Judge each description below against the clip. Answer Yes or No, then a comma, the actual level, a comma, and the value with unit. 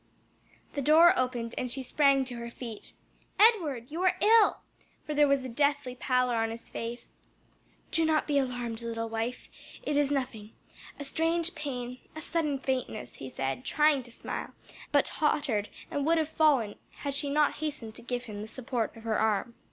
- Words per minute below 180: No, average, 185 wpm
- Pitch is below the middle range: No, very high, 260 Hz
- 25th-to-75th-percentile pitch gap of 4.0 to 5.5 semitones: Yes, average, 4.3 semitones